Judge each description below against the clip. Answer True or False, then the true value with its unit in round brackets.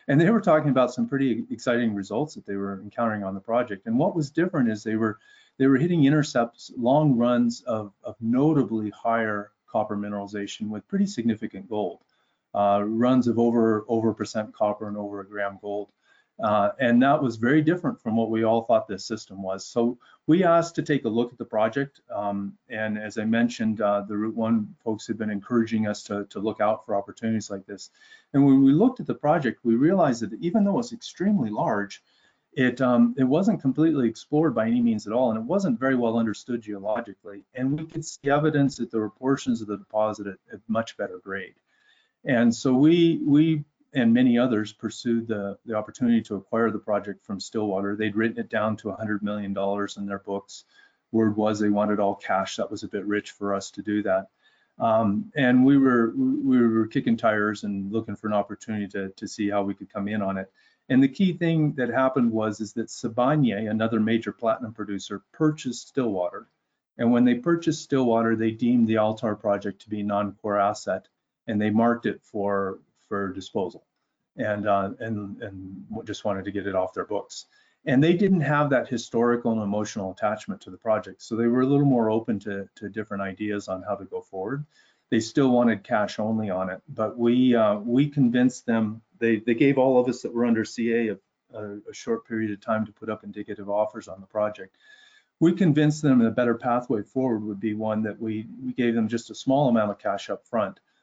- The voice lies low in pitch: True (110 Hz)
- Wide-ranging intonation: False (3.9 semitones)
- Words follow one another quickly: True (210 wpm)